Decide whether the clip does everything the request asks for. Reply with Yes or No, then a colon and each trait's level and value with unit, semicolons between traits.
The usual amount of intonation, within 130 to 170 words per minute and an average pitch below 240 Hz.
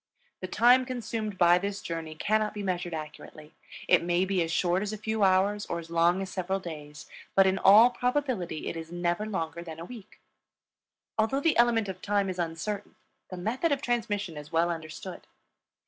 No: average, 4.1 semitones; average, 190 wpm; high, 190 Hz